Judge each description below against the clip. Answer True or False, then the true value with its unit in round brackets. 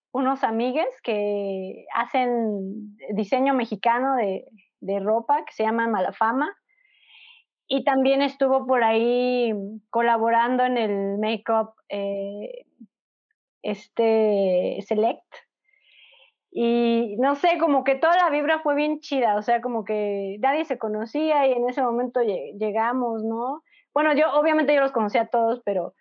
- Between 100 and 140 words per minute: True (135 wpm)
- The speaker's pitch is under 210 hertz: False (240 Hz)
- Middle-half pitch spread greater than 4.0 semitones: True (4.7 semitones)